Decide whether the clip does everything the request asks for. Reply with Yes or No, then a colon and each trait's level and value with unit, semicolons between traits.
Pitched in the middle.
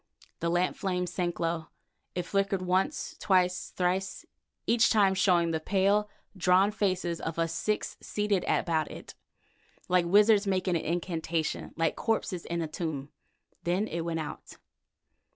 Yes: medium, 180 Hz